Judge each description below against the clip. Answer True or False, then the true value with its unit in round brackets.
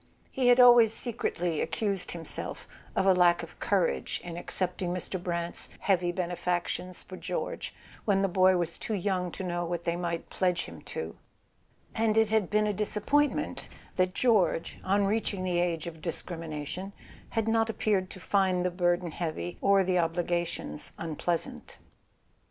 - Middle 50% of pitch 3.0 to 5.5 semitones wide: False (2.6 semitones)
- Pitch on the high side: False (180 Hz)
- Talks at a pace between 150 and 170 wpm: True (165 wpm)